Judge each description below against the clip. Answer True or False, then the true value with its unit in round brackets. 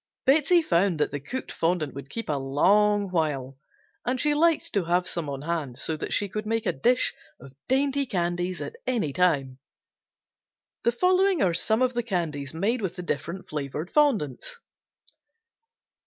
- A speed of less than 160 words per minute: False (170 wpm)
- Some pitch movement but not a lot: False (8.4 semitones)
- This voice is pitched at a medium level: True (180 Hz)